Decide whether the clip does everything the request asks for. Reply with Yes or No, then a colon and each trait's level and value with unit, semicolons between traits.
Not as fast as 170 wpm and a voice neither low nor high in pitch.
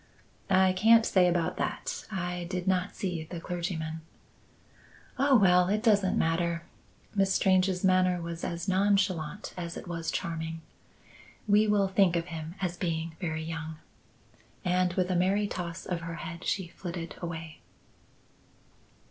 Yes: average, 145 wpm; medium, 180 Hz